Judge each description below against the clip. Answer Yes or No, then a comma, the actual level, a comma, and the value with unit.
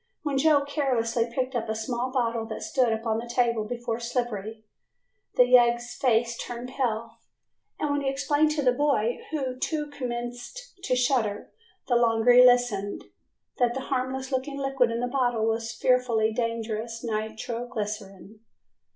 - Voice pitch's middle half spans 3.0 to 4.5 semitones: No, narrow, 2.4 semitones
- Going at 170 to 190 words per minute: No, average, 155 wpm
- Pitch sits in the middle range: No, high, 240 Hz